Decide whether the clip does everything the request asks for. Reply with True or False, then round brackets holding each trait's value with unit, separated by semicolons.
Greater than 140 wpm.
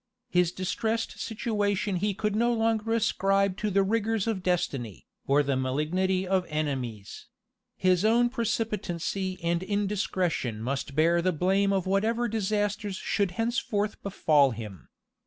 False (135 wpm)